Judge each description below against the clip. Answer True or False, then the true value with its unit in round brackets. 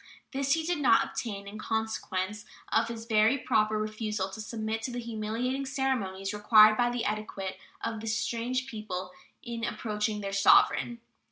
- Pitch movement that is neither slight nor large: False (2.1 semitones)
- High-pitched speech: True (220 Hz)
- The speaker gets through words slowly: False (160 wpm)